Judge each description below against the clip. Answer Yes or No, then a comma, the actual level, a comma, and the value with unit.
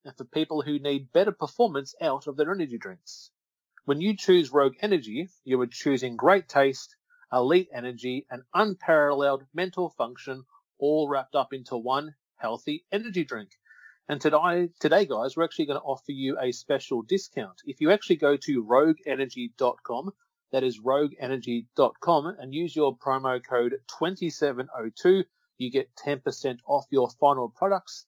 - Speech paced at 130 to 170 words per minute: Yes, average, 150 wpm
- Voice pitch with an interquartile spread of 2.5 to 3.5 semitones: No, wide, 5.4 semitones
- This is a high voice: No, medium, 145 Hz